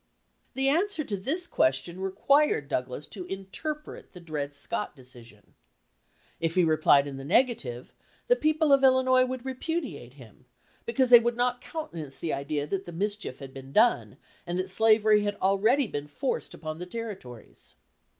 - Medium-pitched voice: No, high, 195 Hz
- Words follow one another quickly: No, average, 160 wpm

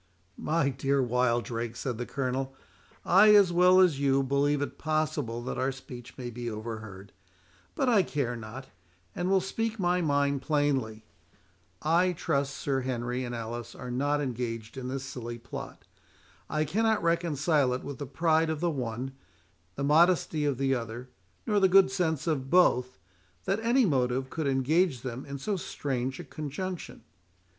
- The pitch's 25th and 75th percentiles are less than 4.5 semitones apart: No, average, 4.9 semitones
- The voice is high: No, medium, 140 Hz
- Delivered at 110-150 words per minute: No, average, 165 wpm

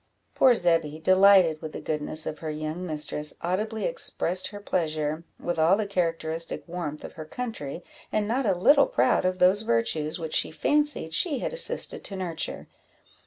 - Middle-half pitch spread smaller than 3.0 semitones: No, average, 4.5 semitones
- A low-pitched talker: No, medium, 175 Hz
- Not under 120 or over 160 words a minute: No, average, 170 wpm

